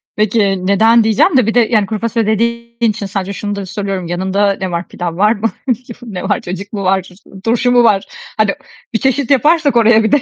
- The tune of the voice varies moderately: Yes, average, 3.2 semitones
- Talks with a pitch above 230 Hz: No, high, 215 Hz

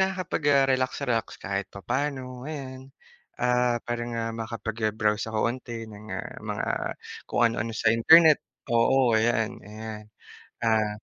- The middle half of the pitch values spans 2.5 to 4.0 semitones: Yes, average, 2.9 semitones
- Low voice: Yes, low, 115 Hz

